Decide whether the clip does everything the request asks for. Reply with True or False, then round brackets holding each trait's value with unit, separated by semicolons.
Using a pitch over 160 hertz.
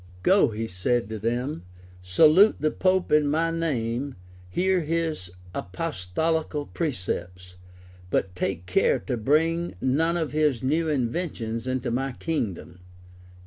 False (140 Hz)